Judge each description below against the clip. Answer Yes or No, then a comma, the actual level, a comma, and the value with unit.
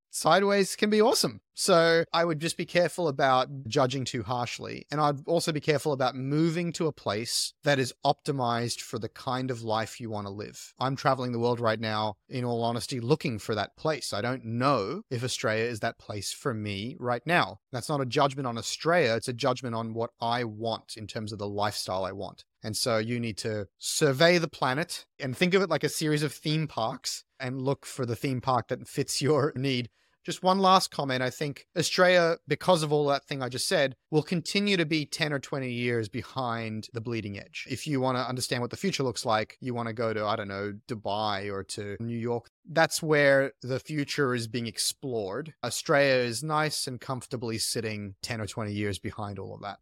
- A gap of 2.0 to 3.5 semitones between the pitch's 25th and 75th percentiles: No, average, 4.9 semitones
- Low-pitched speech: Yes, low, 125 Hz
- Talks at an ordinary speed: No, fast, 215 wpm